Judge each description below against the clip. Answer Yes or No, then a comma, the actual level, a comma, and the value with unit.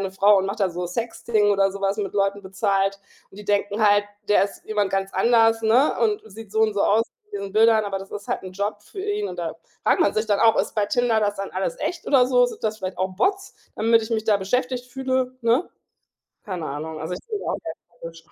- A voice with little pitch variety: No, average, 3.0 semitones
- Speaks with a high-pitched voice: Yes, high, 210 Hz